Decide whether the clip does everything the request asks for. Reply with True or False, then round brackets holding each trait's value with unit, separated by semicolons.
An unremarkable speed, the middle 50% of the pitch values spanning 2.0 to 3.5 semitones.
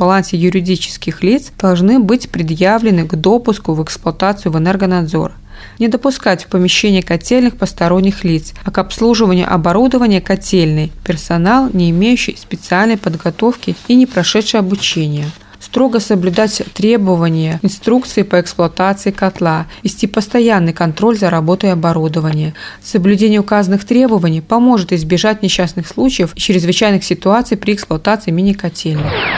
False (120 wpm; 4.0 semitones)